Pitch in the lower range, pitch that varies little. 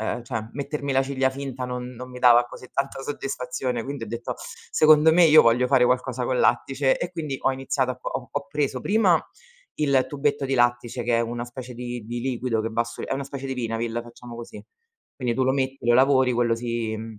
Yes: low, 125 Hz; narrow, 2.3 semitones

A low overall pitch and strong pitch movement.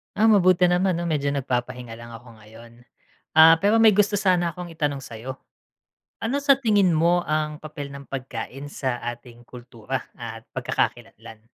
No: medium, 145 Hz; wide, 6.7 semitones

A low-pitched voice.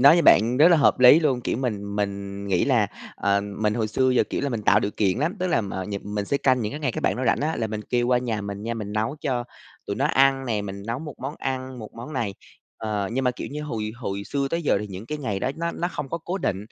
Yes: low, 120 Hz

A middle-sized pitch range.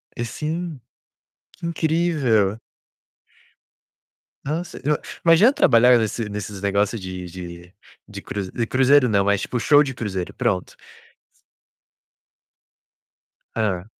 No: wide, 7.0 semitones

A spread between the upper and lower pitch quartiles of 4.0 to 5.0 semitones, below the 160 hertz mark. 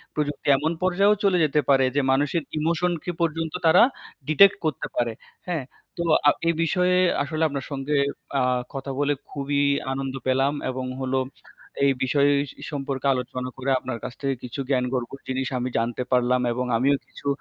No: average, 3.2 semitones; medium, 140 Hz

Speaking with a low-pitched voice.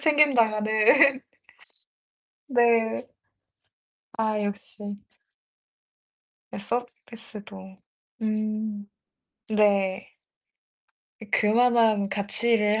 No: high, 215 Hz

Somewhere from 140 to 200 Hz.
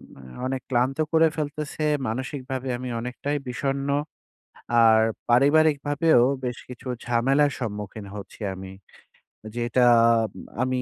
No: low, 130 Hz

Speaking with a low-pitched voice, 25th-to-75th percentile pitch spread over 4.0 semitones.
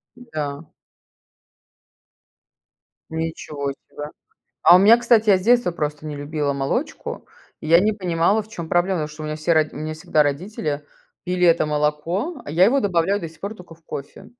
No: medium, 165 Hz; average, 4.4 semitones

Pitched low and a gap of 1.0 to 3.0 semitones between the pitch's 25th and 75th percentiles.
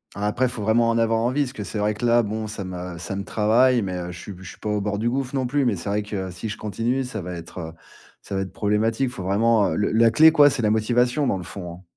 No: low, 110 Hz; average, 3.5 semitones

